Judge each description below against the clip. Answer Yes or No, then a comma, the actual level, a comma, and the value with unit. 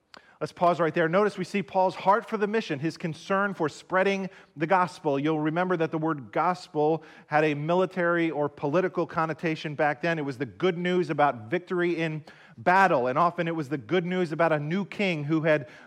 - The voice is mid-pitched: Yes, medium, 170 Hz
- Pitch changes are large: No, average, 2.9 semitones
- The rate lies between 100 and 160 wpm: No, fast, 205 wpm